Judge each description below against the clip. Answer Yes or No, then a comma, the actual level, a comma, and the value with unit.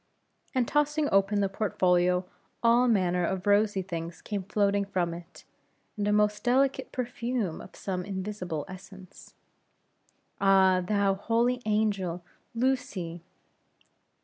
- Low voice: No, high, 200 Hz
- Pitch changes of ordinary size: Yes, average, 3.2 semitones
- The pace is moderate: No, slow, 120 wpm